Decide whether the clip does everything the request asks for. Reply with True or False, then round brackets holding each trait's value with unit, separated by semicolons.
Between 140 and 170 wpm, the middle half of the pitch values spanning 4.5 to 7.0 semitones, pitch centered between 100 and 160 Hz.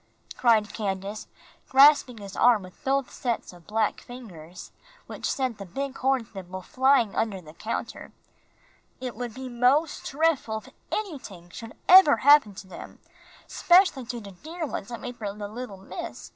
False (160 wpm; 5.1 semitones; 235 Hz)